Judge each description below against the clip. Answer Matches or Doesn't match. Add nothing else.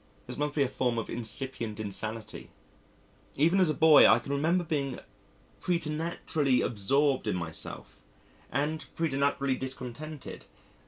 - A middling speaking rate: Doesn't match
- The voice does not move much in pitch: Doesn't match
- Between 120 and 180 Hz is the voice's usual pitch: Matches